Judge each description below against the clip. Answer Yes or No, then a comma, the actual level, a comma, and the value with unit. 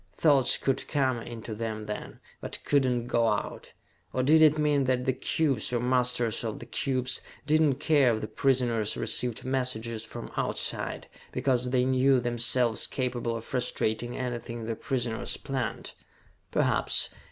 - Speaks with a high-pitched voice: No, low, 125 Hz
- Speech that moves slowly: No, average, 165 wpm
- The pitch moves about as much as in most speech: No, narrow, 2.3 semitones